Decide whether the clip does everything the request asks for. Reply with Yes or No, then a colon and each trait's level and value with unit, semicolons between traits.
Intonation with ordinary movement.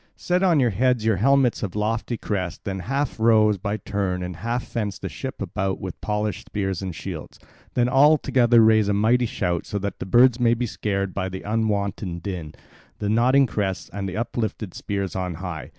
Yes: average, 3.7 semitones